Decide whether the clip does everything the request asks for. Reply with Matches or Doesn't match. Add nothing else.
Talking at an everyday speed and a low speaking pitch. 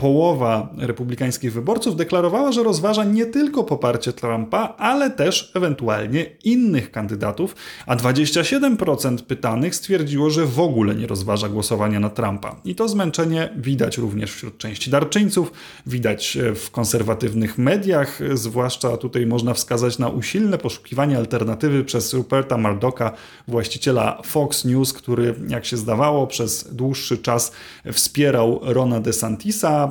Matches